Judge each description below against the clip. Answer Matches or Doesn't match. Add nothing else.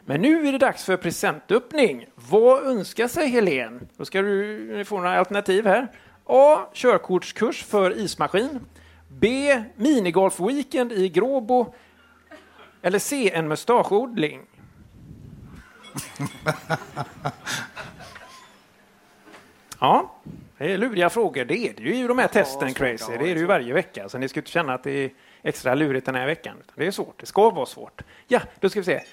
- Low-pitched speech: Doesn't match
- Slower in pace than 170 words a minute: Matches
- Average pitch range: Doesn't match